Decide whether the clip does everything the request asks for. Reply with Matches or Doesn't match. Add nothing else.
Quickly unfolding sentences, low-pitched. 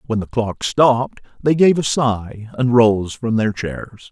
Doesn't match